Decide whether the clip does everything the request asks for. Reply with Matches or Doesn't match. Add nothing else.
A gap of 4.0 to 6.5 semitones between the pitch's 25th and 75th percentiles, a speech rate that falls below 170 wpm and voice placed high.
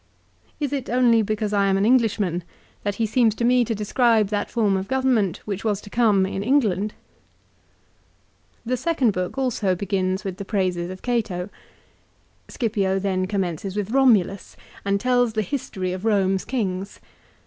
Doesn't match